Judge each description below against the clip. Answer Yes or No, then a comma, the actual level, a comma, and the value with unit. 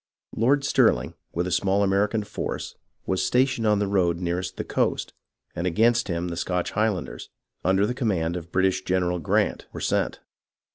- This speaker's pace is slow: No, average, 175 wpm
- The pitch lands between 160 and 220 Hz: No, very low, 95 Hz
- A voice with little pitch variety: No, average, 3.3 semitones